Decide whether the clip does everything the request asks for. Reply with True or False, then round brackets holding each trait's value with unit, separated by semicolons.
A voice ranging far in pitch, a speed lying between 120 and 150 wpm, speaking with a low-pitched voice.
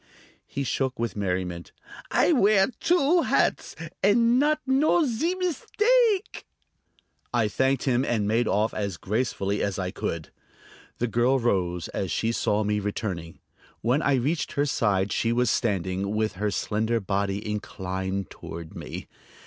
True (6.8 semitones; 145 wpm; 110 Hz)